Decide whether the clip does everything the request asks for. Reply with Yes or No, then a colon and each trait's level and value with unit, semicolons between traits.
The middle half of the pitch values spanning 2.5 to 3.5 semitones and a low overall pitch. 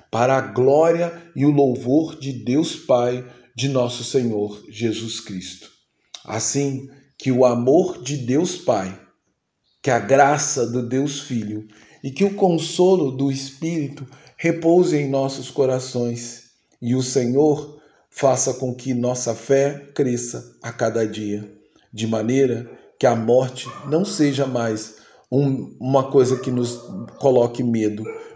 Yes: average, 2.9 semitones; low, 130 Hz